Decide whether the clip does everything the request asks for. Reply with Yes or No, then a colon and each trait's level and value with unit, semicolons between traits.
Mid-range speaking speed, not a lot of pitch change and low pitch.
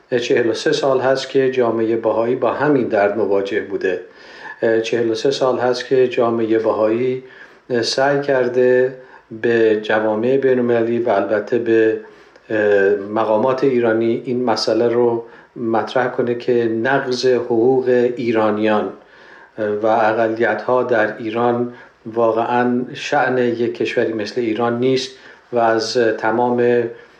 Yes: average, 115 wpm; narrow, 2.3 semitones; low, 120 Hz